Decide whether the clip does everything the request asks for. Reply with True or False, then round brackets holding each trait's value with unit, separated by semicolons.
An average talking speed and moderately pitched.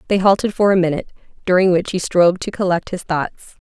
False (210 wpm; 180 Hz)